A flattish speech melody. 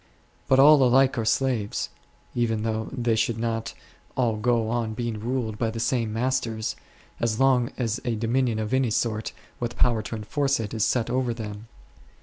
Yes: narrow, 2.3 semitones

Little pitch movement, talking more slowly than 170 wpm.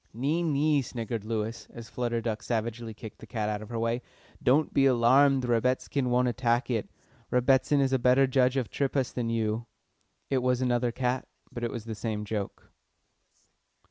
No: narrow, 2.3 semitones; average, 175 wpm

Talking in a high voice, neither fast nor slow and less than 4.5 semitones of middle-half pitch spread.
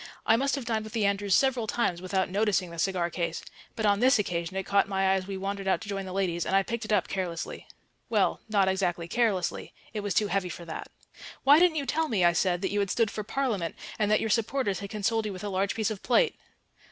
No: high, 200 Hz; fast, 255 wpm; average, 2.8 semitones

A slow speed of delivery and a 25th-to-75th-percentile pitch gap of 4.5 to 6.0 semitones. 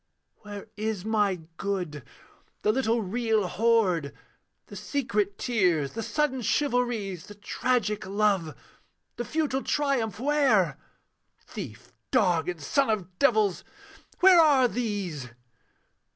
Yes: slow, 110 wpm; average, 5.0 semitones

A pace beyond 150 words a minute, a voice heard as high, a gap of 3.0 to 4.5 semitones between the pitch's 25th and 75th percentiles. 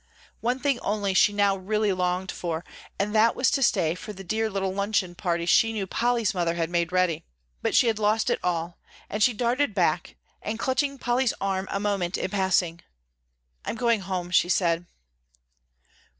Yes: average, 180 wpm; high, 195 Hz; average, 3.8 semitones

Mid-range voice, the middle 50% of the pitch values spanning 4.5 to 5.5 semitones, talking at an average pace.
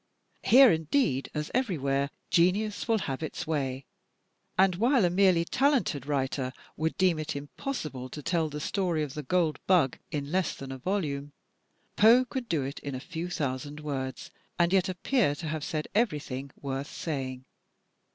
Yes: medium, 155 Hz; average, 5.1 semitones; average, 165 wpm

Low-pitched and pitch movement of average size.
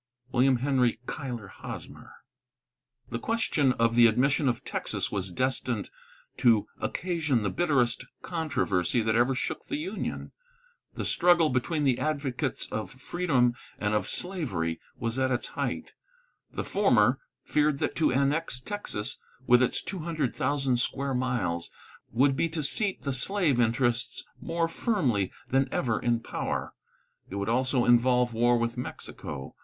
Yes: low, 130 Hz; average, 4.0 semitones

